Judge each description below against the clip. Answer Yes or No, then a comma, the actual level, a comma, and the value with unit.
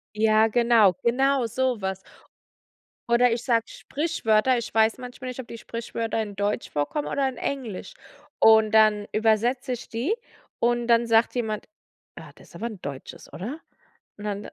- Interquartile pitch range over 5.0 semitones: No, narrow, 2.5 semitones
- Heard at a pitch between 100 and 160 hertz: No, high, 230 Hz